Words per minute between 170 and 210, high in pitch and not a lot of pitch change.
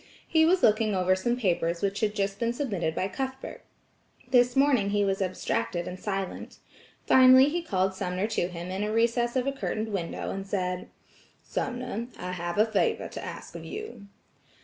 No: average, 180 wpm; high, 205 Hz; average, 4.7 semitones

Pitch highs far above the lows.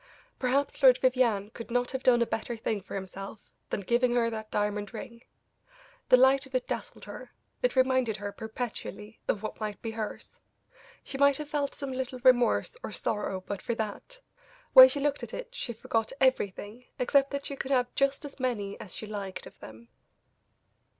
No: average, 4.0 semitones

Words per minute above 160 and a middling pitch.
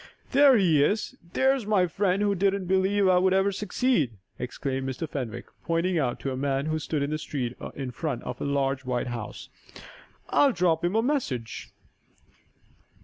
Yes: average, 170 wpm; medium, 165 Hz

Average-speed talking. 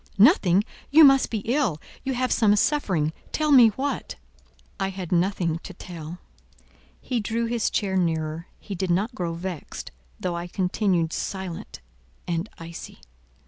Yes: average, 145 wpm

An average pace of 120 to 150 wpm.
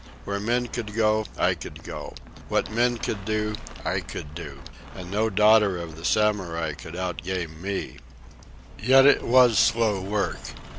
No: average, 160 wpm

